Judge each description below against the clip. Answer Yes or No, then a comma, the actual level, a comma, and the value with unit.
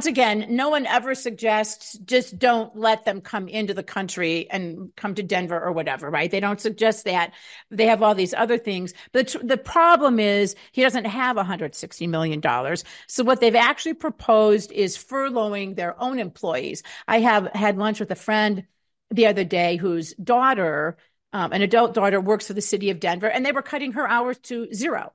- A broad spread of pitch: No, average, 4.0 semitones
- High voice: Yes, high, 215 Hz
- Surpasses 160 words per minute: Yes, average, 190 wpm